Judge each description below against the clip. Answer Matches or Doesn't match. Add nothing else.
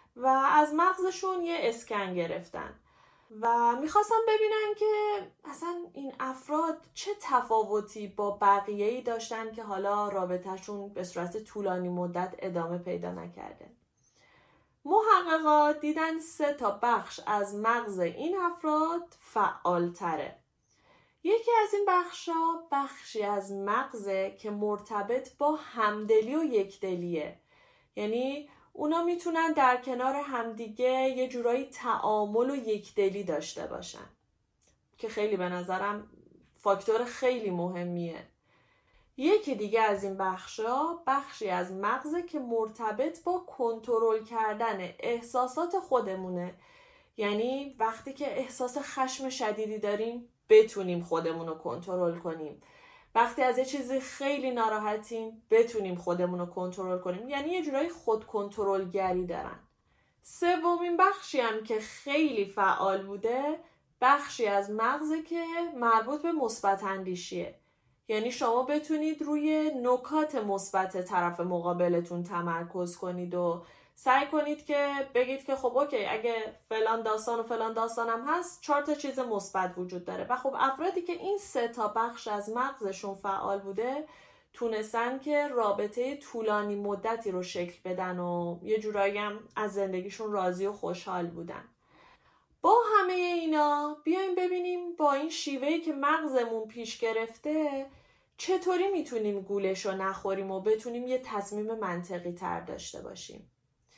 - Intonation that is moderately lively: Doesn't match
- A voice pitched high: Matches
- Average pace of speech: Matches